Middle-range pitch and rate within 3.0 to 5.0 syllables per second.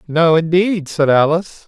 Yes: medium, 165 Hz; 4.6 syllables/s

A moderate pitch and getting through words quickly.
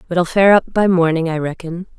Yes: medium, 175 Hz; fast, 210 wpm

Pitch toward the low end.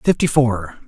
Yes: low, 125 Hz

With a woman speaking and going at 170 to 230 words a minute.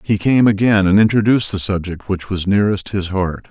No: male; fast, 205 wpm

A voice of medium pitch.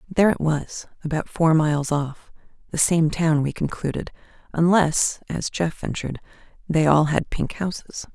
Yes: medium, 160 Hz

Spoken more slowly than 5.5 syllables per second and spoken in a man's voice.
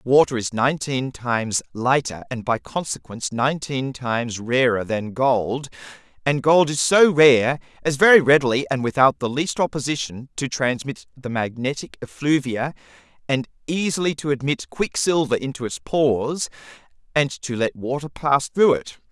Yes: 4.8 syllables/s; male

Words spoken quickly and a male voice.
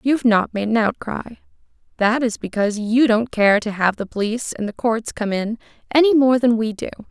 No: fast, 220 wpm; female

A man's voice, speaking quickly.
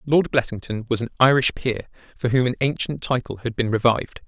No: male; average, 195 wpm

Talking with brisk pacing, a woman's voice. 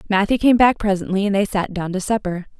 Yes: fast, 230 wpm; female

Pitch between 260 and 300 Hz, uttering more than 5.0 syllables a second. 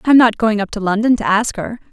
No: high, 220 Hz; 5.8 syllables/s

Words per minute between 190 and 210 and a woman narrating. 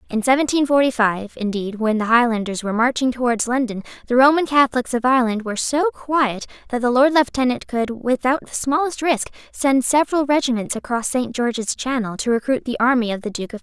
Yes: average, 200 wpm; female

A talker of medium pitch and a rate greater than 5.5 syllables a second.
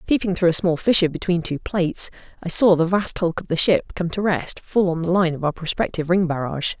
Yes: medium, 175 Hz; 6.0 syllables/s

